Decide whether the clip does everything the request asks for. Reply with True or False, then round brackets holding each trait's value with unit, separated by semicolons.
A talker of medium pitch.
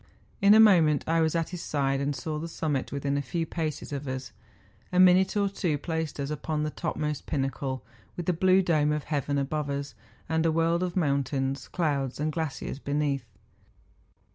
True (150 Hz)